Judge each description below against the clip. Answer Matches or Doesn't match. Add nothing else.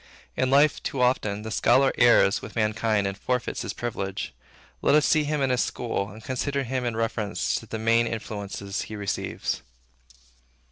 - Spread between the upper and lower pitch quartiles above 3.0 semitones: Matches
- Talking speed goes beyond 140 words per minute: Matches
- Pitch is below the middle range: Matches